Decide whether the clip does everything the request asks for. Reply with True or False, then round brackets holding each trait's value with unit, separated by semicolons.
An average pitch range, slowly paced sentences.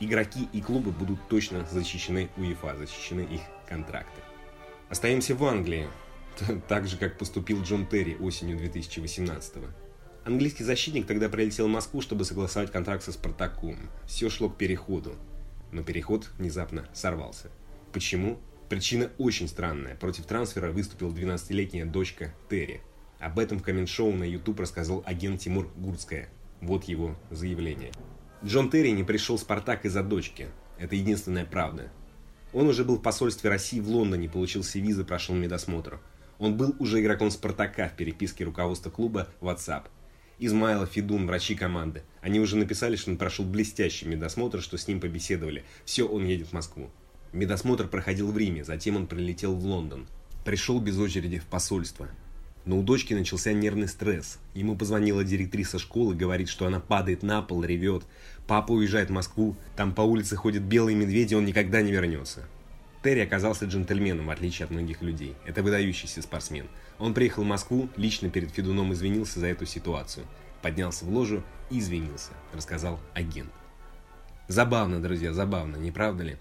False (3.8 semitones; 155 wpm)